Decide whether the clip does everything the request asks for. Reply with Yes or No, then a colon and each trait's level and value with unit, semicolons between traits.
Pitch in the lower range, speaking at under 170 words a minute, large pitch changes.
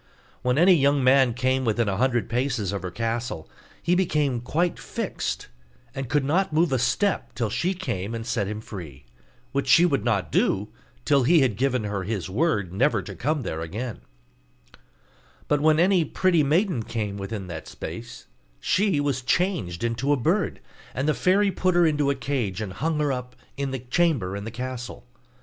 No: low, 130 Hz; average, 185 wpm; wide, 5.9 semitones